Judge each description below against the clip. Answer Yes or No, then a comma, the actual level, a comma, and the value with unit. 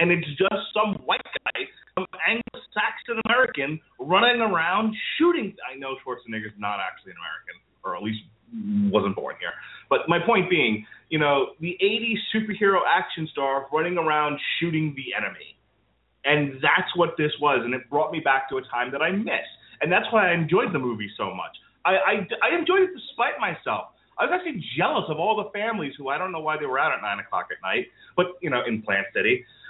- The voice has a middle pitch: Yes, medium, 165 Hz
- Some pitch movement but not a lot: No, wide, 7.3 semitones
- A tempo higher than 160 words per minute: Yes, fast, 205 wpm